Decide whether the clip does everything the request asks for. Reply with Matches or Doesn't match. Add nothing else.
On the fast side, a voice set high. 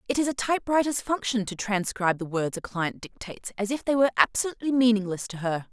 Matches